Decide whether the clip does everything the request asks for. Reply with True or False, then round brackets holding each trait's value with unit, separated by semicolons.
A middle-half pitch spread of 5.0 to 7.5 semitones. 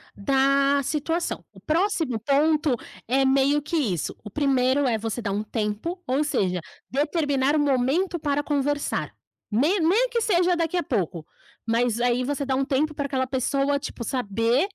False (3.6 semitones)